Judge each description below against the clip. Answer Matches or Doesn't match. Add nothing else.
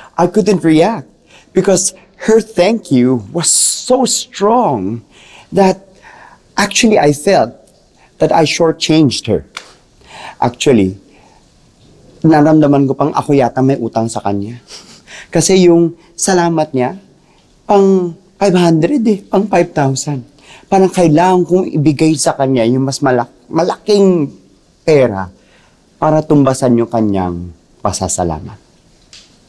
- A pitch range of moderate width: Doesn't match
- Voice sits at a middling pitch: Matches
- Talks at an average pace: Doesn't match